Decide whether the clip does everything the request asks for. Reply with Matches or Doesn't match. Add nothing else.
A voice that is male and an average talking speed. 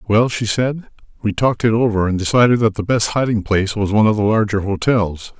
Doesn't match